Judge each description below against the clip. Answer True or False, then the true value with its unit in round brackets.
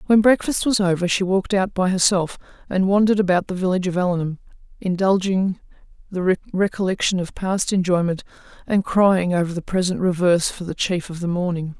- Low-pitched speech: False (185 Hz)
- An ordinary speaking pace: True (175 wpm)